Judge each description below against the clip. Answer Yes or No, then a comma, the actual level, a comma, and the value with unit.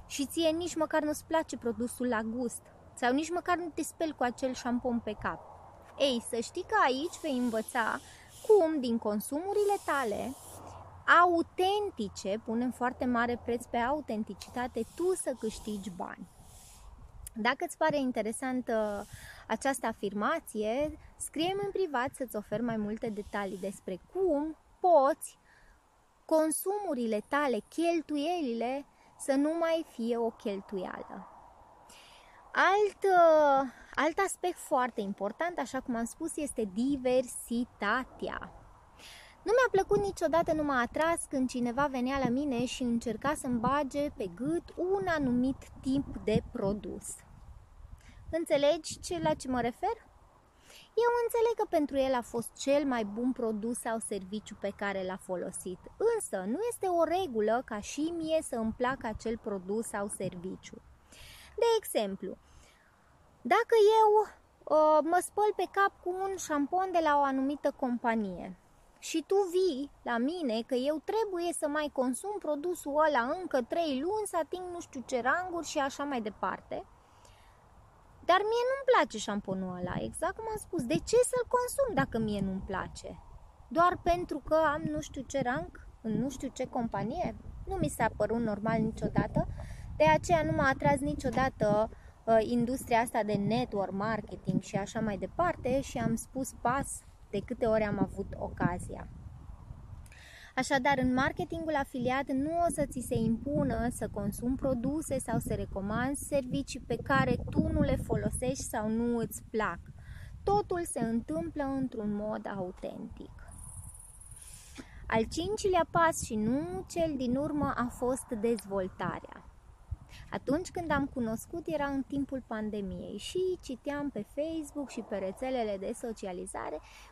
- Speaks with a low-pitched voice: No, very high, 265 Hz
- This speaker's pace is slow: No, average, 145 wpm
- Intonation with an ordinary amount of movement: No, wide, 6.4 semitones